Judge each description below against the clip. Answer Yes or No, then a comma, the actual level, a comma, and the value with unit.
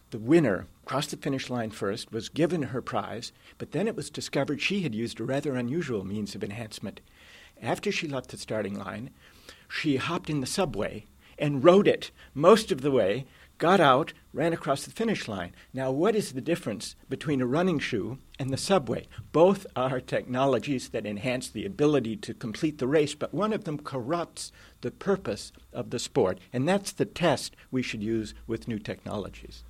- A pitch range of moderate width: No, wide, 6.0 semitones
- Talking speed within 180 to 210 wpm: Yes, average, 190 wpm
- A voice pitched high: No, low, 135 Hz